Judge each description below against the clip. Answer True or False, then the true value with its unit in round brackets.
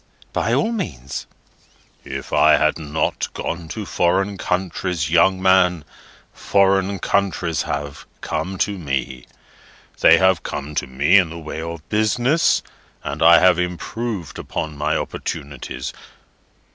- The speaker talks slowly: True (130 wpm)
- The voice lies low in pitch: True (85 Hz)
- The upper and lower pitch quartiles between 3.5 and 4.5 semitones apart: True (3.8 semitones)